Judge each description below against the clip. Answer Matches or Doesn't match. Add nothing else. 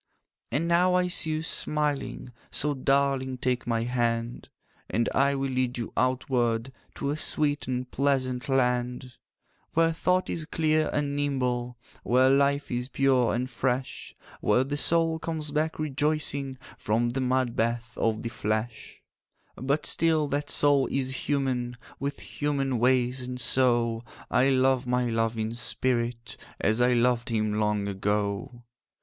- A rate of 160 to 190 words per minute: Doesn't match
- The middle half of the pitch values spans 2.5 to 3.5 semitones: Matches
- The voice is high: Doesn't match